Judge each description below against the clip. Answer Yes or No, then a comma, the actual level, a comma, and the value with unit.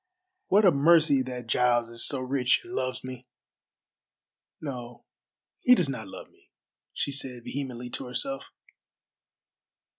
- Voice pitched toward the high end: No, low, 130 Hz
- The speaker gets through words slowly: Yes, slow, 130 wpm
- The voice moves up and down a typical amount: No, narrow, 2.3 semitones